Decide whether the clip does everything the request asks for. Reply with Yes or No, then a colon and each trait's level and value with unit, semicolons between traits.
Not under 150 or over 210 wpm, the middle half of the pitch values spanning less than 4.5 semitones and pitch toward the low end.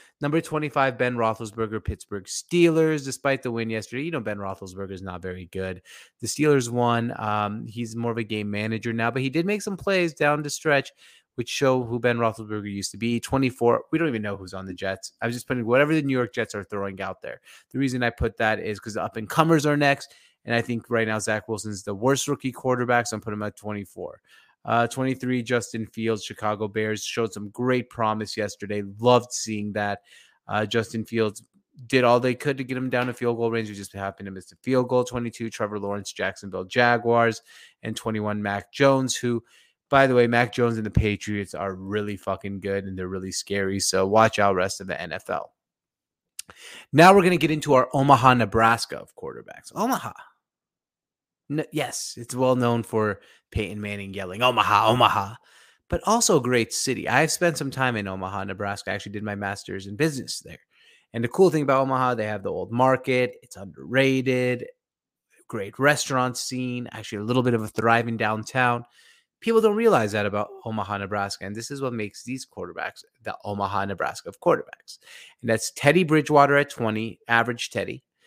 Yes: average, 200 wpm; average, 3.8 semitones; low, 115 Hz